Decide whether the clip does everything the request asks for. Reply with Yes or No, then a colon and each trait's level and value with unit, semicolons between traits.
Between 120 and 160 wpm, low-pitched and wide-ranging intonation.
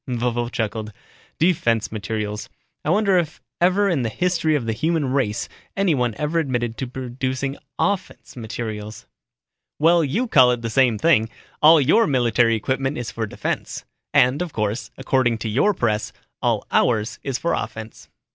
Yes: average, 155 wpm; low, 125 Hz; wide, 5.7 semitones